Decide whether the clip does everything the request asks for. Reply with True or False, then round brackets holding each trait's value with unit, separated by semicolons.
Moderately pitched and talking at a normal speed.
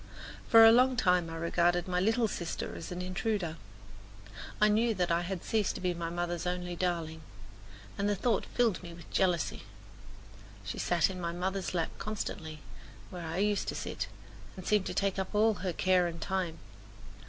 True (180 Hz; 185 wpm)